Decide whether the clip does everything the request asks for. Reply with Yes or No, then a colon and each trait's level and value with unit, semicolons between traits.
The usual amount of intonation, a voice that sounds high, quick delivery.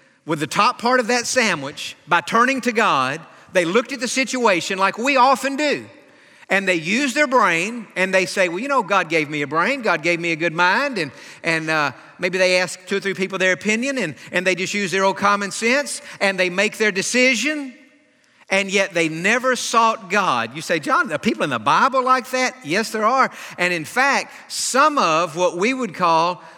No: wide, 6.0 semitones; high, 200 Hz; fast, 215 wpm